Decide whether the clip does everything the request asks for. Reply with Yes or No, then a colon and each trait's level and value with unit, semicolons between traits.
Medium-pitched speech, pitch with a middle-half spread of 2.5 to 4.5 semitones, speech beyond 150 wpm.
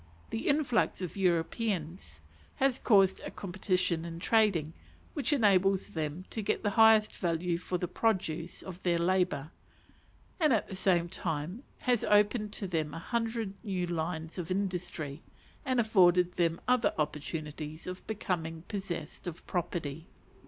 No: medium, 180 Hz; average, 4.1 semitones; average, 145 wpm